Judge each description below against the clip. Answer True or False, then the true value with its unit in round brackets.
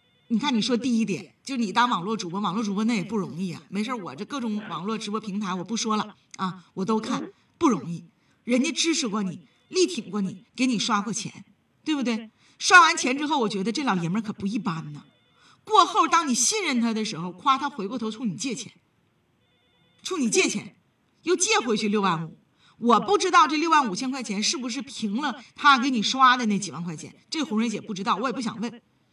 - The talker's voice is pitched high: True (225 Hz)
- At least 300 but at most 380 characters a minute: True (310 characters per minute)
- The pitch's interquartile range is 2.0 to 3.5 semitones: False (4.8 semitones)